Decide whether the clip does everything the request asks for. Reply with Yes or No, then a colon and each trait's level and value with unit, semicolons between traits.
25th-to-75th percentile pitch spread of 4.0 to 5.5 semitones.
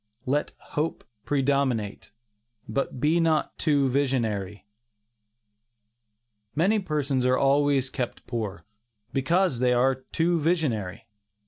No: average, 3.6 semitones